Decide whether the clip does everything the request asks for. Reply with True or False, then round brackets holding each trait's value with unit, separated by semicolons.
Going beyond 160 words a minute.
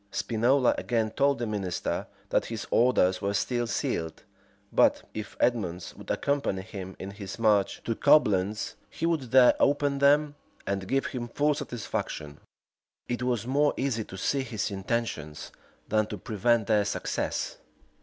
False (150 wpm)